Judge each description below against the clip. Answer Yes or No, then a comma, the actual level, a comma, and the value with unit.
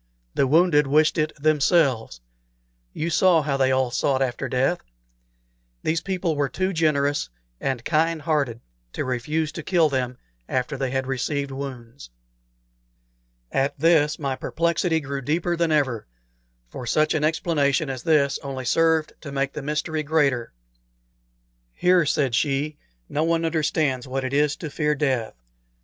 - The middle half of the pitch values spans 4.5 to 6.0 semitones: No, average, 3.1 semitones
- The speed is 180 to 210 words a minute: No, average, 150 wpm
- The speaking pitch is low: No, medium, 145 Hz